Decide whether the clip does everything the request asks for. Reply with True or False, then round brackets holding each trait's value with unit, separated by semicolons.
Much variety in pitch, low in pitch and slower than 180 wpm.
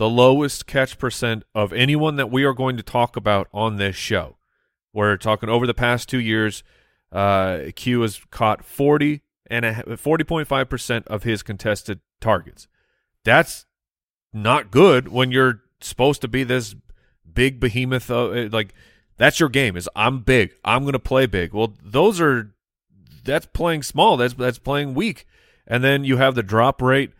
False (3.5 semitones; 120 Hz; 170 wpm)